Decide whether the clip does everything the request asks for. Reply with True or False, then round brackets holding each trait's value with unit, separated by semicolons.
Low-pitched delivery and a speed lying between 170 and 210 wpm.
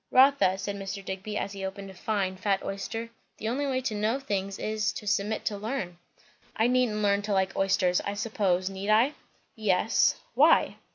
False (205 Hz; 185 wpm)